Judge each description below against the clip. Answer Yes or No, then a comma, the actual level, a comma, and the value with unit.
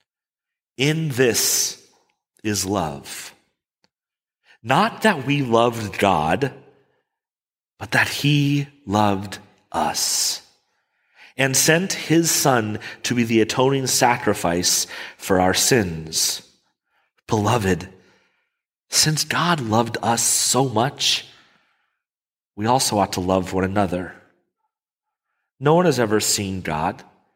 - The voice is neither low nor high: No, low, 115 Hz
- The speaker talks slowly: Yes, slow, 100 wpm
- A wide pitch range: Yes, wide, 6.4 semitones